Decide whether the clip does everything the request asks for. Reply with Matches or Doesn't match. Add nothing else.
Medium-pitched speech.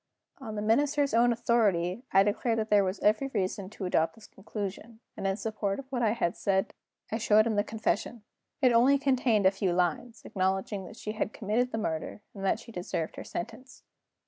Doesn't match